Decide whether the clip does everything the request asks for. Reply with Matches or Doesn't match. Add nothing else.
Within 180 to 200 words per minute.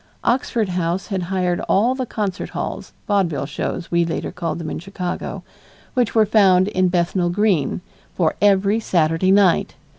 Doesn't match